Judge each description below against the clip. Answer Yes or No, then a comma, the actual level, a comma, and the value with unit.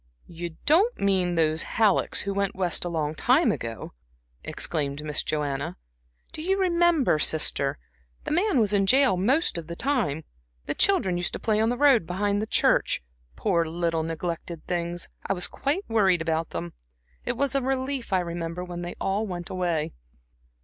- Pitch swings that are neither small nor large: No, wide, 6.9 semitones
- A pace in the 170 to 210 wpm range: Yes, average, 175 wpm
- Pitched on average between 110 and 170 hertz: No, medium, 180 Hz